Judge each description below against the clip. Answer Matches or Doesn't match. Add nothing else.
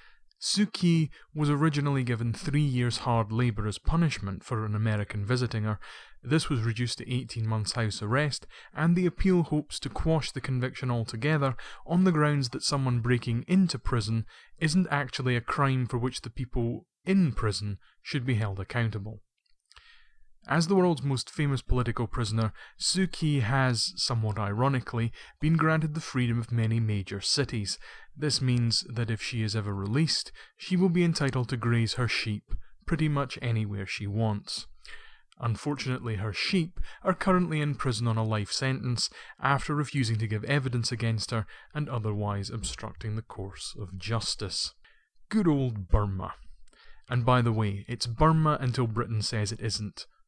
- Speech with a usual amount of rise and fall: Matches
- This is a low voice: Matches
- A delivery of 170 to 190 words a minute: Doesn't match